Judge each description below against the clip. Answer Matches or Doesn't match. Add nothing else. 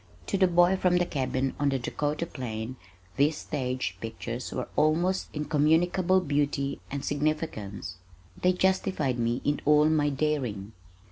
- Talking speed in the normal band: Matches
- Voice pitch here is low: Doesn't match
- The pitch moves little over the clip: Doesn't match